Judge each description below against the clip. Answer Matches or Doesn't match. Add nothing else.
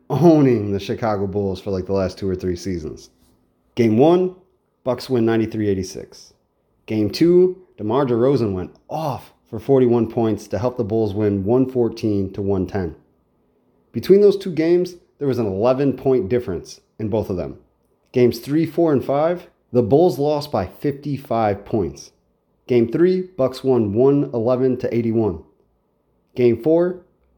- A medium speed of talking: Matches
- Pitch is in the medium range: Doesn't match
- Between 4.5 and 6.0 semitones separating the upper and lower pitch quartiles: Matches